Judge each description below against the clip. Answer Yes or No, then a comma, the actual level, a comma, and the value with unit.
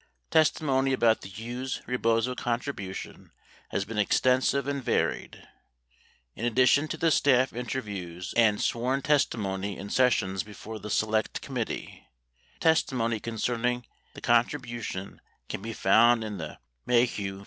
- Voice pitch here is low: Yes, low, 115 Hz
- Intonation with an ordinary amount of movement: Yes, average, 3.6 semitones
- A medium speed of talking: No, slow, 130 wpm